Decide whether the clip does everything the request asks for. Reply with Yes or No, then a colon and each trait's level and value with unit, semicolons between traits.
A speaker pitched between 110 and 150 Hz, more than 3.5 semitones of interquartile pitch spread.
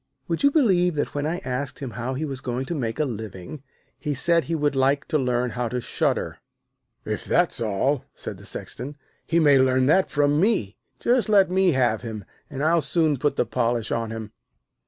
Yes: medium, 140 Hz; average, 4.7 semitones